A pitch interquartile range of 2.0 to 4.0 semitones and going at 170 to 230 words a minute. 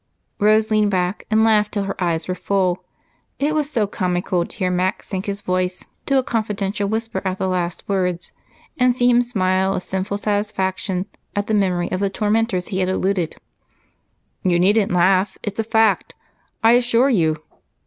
Yes: average, 2.9 semitones; average, 180 wpm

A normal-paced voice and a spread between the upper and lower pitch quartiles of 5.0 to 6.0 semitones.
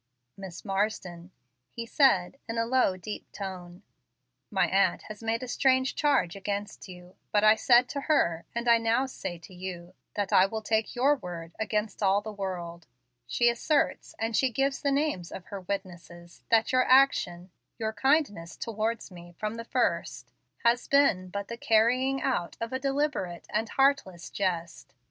Yes: average, 170 wpm; average, 5.3 semitones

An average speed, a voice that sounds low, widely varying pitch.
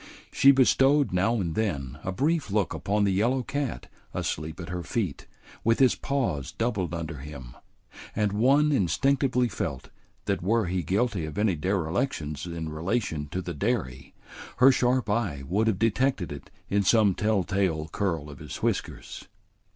Yes: average, 160 wpm; low, 100 Hz; wide, 6.6 semitones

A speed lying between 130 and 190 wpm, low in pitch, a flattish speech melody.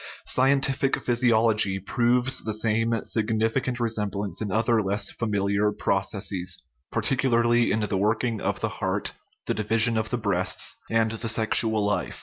Yes: average, 140 wpm; low, 110 Hz; narrow, 2.2 semitones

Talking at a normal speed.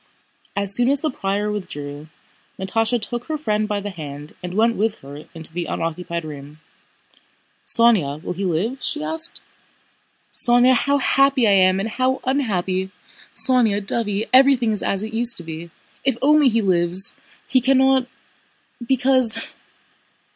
Yes: average, 150 wpm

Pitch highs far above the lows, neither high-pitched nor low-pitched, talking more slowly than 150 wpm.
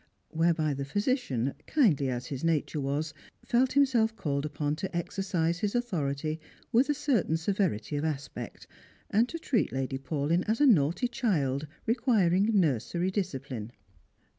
Yes: wide, 7.7 semitones; medium, 165 Hz; average, 140 wpm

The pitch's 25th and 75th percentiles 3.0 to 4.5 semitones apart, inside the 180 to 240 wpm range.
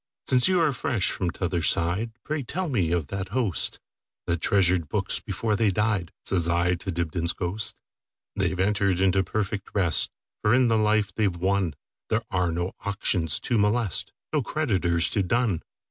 No: average, 4.0 semitones; average, 150 wpm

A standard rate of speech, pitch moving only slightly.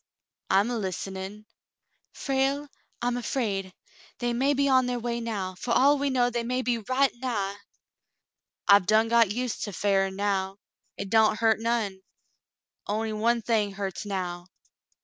No: average, 150 wpm; average, 3.6 semitones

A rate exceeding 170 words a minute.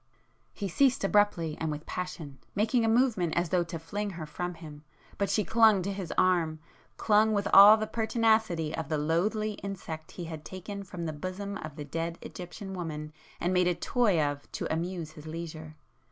Yes: average, 180 wpm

